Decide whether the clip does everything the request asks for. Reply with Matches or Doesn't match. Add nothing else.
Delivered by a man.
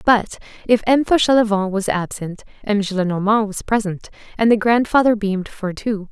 Doesn't match